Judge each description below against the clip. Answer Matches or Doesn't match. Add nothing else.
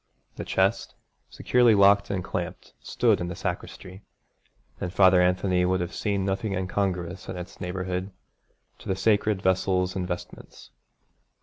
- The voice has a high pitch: Doesn't match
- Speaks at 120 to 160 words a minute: Matches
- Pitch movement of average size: Doesn't match